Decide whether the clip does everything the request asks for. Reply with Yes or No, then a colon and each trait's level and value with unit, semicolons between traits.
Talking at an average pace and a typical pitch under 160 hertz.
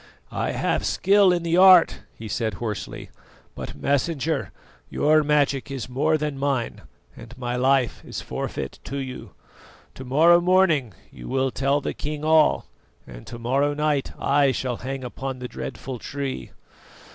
Yes: average, 155 wpm; medium, 140 Hz